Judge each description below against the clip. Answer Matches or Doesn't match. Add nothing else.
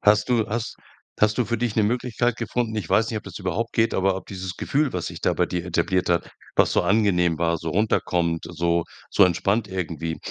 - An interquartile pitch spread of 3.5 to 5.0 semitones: Matches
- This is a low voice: Matches